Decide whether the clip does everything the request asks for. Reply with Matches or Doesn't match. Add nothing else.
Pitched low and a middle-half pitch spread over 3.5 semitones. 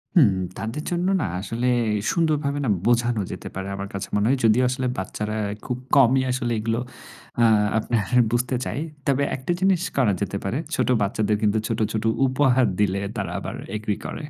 Matches